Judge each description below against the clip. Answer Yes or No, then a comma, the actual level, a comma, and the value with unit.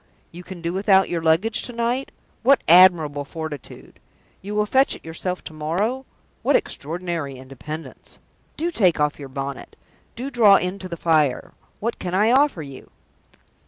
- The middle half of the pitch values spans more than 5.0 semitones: Yes, wide, 5.4 semitones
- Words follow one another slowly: No, average, 160 wpm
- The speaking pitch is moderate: Yes, medium, 175 Hz